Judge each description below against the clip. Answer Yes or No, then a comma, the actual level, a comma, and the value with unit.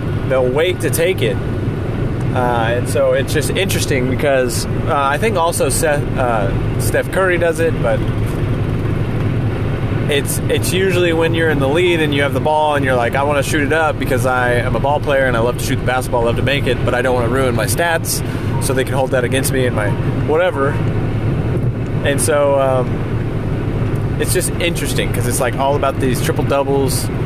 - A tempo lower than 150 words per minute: No, fast, 205 wpm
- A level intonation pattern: Yes, narrow, 2.2 semitones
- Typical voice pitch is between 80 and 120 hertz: No, low, 130 Hz